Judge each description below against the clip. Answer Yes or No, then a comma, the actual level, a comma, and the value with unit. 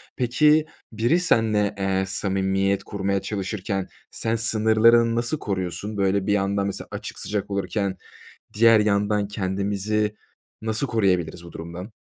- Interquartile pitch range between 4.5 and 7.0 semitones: No, narrow, 2.4 semitones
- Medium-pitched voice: No, low, 100 Hz